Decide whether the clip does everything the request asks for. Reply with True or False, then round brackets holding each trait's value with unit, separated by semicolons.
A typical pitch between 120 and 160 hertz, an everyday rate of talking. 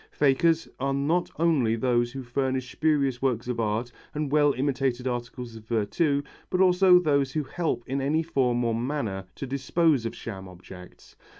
True (135 Hz; 170 wpm)